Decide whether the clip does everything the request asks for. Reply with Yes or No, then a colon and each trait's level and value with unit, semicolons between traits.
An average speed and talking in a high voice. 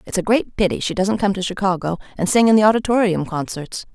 No: fast, 230 wpm; high, 195 Hz